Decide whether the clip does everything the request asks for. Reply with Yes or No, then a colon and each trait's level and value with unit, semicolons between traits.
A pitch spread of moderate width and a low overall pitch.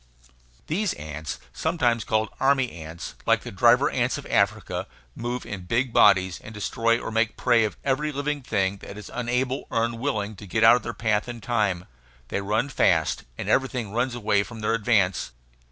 Yes: average, 3.5 semitones; low, 115 Hz